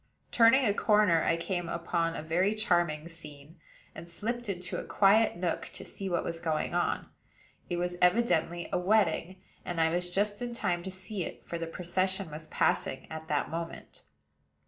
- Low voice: No, medium, 175 Hz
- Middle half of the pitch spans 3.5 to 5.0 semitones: No, average, 3.1 semitones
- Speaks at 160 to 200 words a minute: Yes, average, 180 wpm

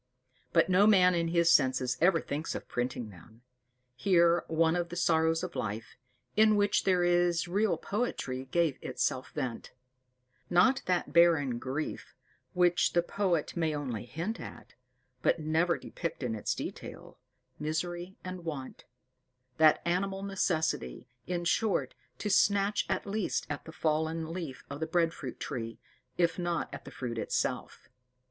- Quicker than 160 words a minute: No, average, 150 wpm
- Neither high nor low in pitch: Yes, medium, 170 Hz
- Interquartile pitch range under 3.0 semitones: No, average, 3.7 semitones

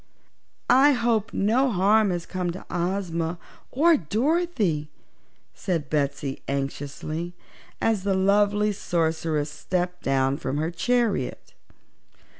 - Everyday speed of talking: No, slow, 105 wpm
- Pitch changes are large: Yes, wide, 5.7 semitones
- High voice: No, medium, 180 Hz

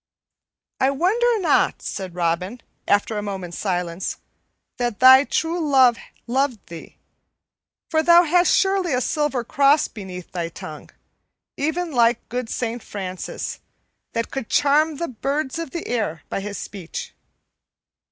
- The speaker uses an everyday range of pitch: No, wide, 7.5 semitones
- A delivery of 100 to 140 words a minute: Yes, slow, 135 wpm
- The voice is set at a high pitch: Yes, very high, 250 Hz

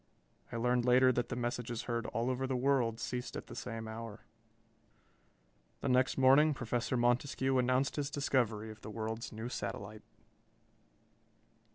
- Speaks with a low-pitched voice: Yes, low, 120 Hz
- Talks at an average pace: Yes, average, 150 wpm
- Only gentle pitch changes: Yes, narrow, 2.3 semitones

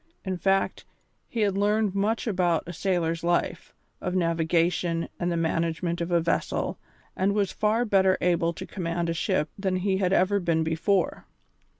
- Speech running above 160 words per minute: Yes, average, 170 wpm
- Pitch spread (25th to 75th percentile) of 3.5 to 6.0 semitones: No, average, 2.7 semitones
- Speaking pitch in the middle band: Yes, medium, 180 Hz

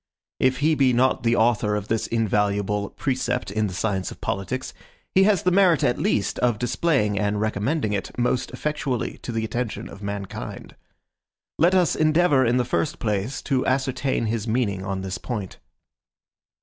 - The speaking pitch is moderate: No, low, 120 Hz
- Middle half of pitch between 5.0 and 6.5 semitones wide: No, average, 4.2 semitones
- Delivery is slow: No, average, 170 wpm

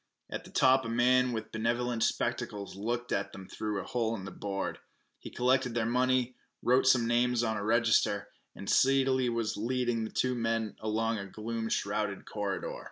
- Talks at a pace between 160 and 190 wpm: Yes, average, 180 wpm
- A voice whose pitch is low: Yes, low, 115 Hz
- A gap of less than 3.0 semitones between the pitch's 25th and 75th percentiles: Yes, narrow, 2.5 semitones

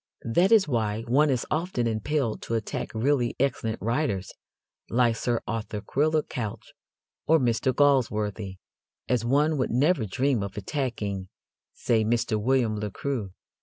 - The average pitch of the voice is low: Yes, low, 120 Hz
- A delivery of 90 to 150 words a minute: Yes, average, 140 wpm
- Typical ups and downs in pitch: Yes, average, 4.4 semitones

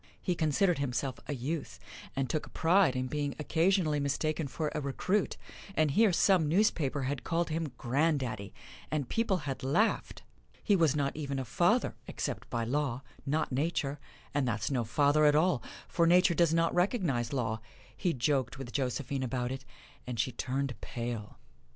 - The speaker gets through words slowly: No, average, 170 wpm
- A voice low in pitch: No, medium, 145 Hz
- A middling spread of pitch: Yes, average, 4.1 semitones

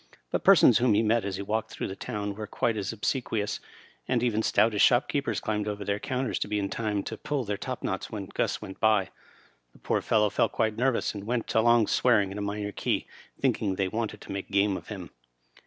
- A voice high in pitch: No, low, 105 Hz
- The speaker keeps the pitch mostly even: Yes, narrow, 2.3 semitones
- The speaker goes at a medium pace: No, fast, 225 wpm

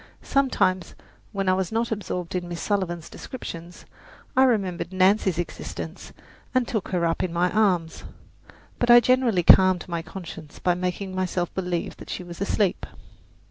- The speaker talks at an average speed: Yes, average, 155 wpm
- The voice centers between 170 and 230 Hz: Yes, medium, 185 Hz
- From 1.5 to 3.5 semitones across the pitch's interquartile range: Yes, average, 2.9 semitones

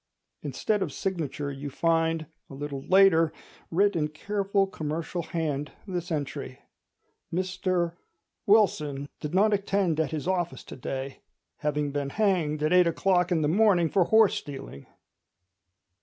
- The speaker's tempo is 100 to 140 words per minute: Yes, slow, 135 wpm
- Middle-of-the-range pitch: Yes, medium, 165 Hz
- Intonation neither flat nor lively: Yes, average, 4.2 semitones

